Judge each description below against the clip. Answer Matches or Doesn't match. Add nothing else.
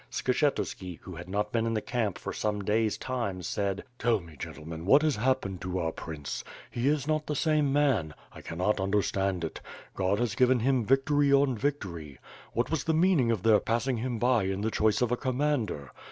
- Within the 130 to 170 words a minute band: Doesn't match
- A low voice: Matches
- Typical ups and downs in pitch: Doesn't match